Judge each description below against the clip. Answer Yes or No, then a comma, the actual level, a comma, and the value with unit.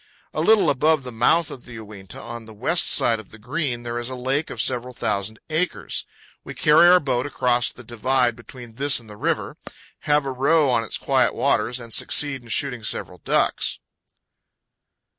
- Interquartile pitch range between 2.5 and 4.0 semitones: Yes, average, 3.6 semitones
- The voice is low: Yes, low, 125 Hz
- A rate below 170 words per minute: No, average, 190 wpm